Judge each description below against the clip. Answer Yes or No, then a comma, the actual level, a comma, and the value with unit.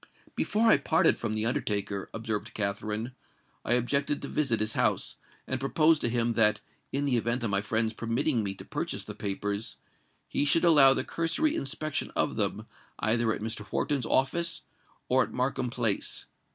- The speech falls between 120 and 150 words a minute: No, average, 175 wpm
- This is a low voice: Yes, low, 120 Hz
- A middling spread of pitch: Yes, average, 4.3 semitones